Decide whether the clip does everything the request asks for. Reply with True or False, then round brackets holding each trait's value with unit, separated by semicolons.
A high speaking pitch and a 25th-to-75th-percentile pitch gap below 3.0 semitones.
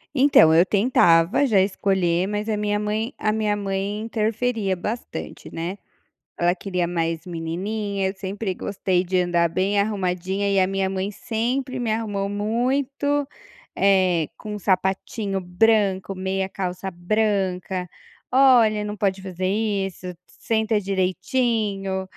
True (195 Hz; 2.6 semitones)